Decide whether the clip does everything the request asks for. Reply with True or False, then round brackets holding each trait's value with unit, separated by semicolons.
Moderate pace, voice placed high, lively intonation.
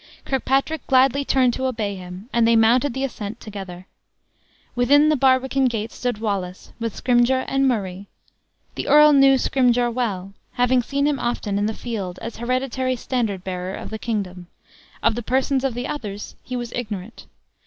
False (170 wpm; 240 Hz; 4.0 semitones)